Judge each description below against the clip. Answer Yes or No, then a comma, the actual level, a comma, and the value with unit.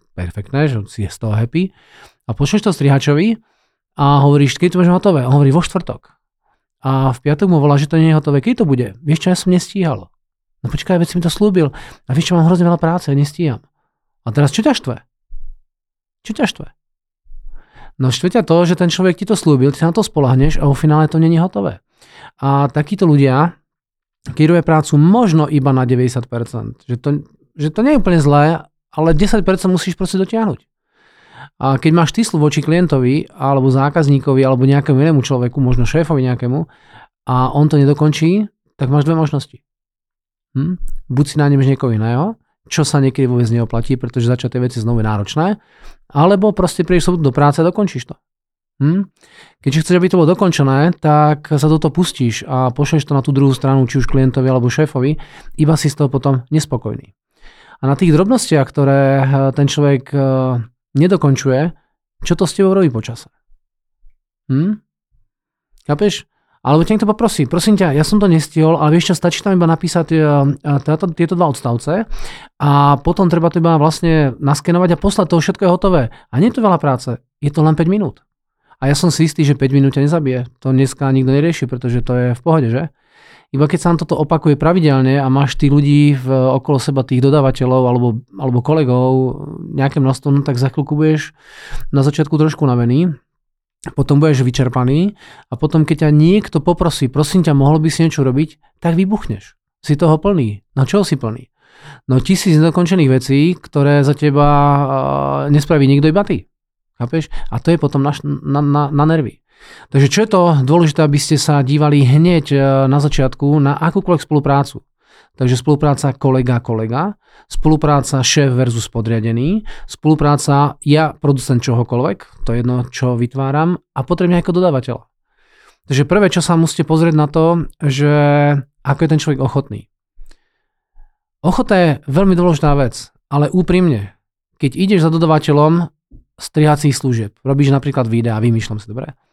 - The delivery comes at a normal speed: No, fast, 175 wpm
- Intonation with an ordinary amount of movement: Yes, average, 3.9 semitones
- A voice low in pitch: No, medium, 145 Hz